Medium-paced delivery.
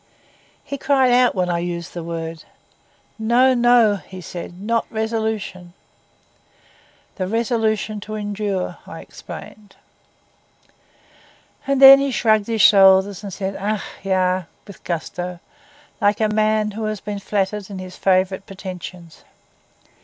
No: slow, 130 wpm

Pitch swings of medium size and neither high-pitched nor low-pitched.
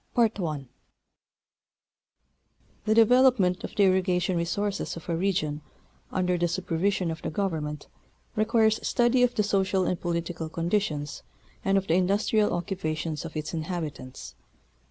Yes: average, 3.7 semitones; medium, 180 Hz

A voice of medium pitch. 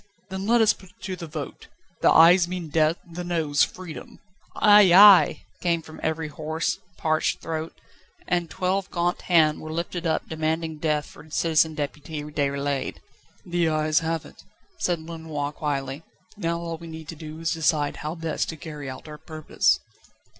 Yes: medium, 160 Hz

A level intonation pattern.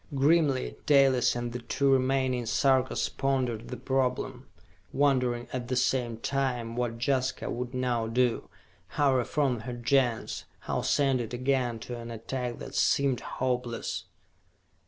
Yes: narrow, 1.9 semitones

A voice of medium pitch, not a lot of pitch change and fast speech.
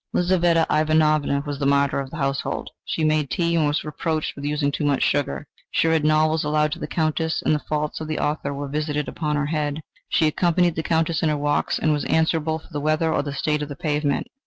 Yes: medium, 150 Hz; narrow, 1.5 semitones; fast, 235 wpm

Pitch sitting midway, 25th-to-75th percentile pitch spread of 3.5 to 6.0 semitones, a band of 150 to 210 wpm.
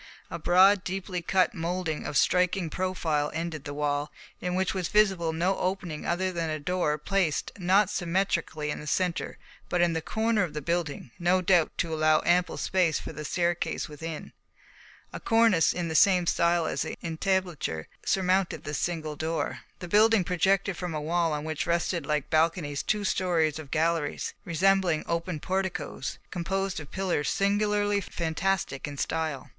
No: medium, 175 Hz; average, 3.1 semitones; average, 165 wpm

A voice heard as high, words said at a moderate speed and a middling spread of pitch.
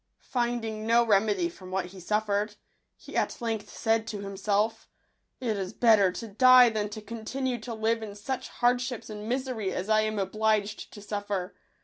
No: high, 215 Hz; average, 170 wpm; narrow, 2.3 semitones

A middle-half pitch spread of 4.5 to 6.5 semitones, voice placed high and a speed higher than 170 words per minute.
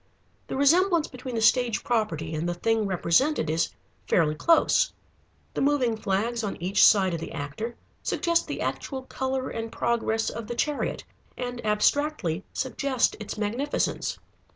No: average, 5.2 semitones; high, 230 Hz; average, 150 wpm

